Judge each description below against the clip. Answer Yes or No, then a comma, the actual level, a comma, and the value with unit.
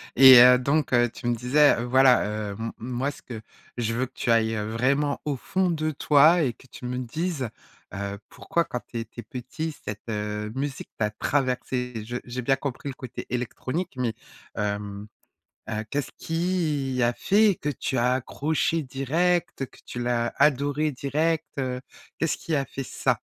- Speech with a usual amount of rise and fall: Yes, average, 3.7 semitones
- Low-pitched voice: Yes, low, 130 Hz